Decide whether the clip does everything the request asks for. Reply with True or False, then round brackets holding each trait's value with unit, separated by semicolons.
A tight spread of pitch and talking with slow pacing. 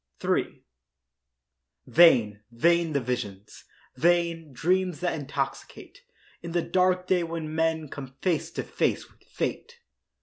False (4.4 semitones; 115 wpm)